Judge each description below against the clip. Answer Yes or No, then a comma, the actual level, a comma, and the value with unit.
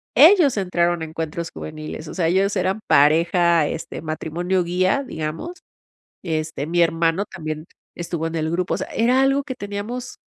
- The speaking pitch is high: No, medium, 175 Hz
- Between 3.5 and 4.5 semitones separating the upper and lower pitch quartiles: Yes, average, 4.1 semitones